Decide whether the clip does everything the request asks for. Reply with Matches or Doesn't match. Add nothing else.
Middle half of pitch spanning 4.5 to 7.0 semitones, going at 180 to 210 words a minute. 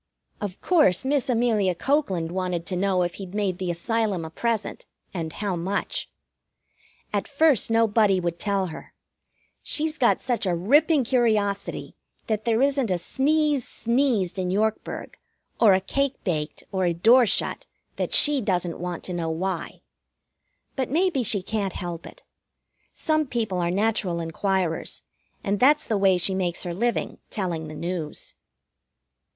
Doesn't match